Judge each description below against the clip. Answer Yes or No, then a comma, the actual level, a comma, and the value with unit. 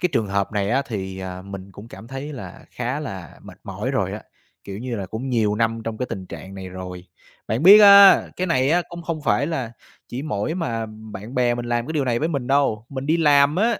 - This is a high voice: No, low, 120 Hz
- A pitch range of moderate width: No, wide, 6.0 semitones